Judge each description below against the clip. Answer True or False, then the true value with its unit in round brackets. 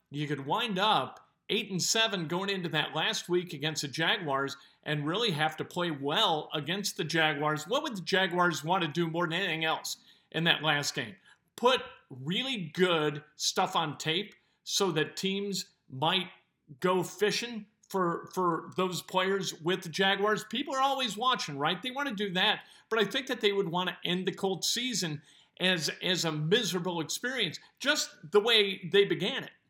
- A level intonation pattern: False (4.4 semitones)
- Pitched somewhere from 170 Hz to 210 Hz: True (185 Hz)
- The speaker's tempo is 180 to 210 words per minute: True (185 wpm)